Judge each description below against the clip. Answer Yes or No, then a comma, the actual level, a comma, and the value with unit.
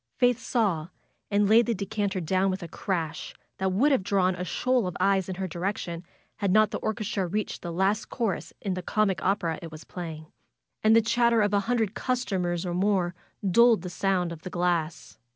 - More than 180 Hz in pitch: Yes, high, 190 Hz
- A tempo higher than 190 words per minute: Yes, average, 200 wpm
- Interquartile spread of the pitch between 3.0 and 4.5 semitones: Yes, average, 3.3 semitones